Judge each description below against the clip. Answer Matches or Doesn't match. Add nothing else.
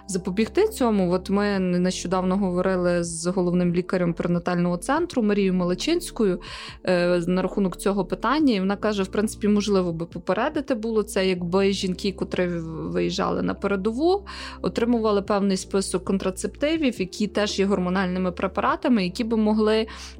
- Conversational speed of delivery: Matches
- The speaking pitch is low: Doesn't match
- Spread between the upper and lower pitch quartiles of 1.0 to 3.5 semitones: Matches